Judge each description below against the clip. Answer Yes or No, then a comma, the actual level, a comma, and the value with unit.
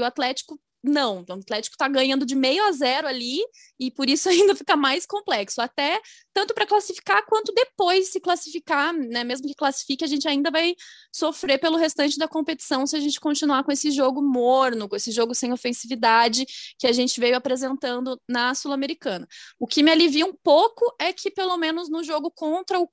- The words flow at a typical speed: No, fast, 195 wpm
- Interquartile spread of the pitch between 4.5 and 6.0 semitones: Yes, average, 4.9 semitones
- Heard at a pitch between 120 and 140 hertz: No, very high, 290 Hz